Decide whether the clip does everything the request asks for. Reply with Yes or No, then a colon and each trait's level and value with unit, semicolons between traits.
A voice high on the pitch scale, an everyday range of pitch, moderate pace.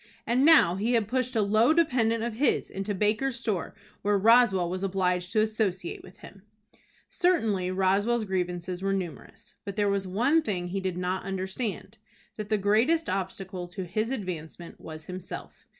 Yes: high, 200 Hz; average, 3.7 semitones; average, 165 wpm